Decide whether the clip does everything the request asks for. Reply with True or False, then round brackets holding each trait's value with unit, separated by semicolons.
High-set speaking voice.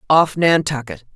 False (150 Hz)